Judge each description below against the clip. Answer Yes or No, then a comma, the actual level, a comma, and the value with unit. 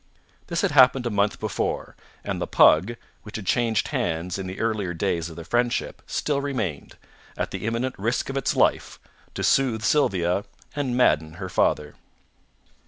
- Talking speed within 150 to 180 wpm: Yes, average, 170 wpm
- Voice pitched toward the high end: No, low, 110 Hz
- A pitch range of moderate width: No, wide, 5.8 semitones